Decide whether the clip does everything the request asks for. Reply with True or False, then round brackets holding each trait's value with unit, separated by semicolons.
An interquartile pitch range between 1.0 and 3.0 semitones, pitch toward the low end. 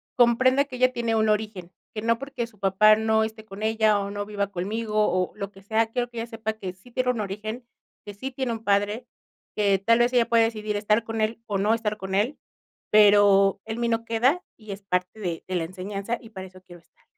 False (2.5 semitones; 215 Hz)